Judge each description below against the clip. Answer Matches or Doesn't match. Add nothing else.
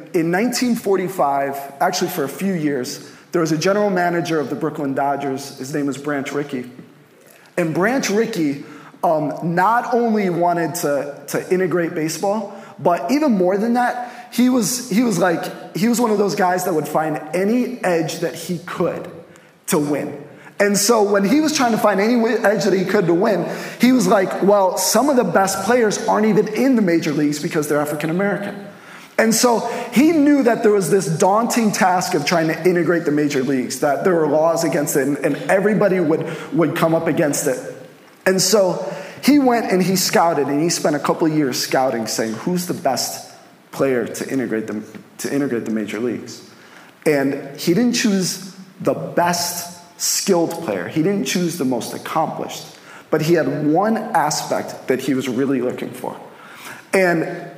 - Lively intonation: Doesn't match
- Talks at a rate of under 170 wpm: Doesn't match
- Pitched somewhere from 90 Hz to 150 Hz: Doesn't match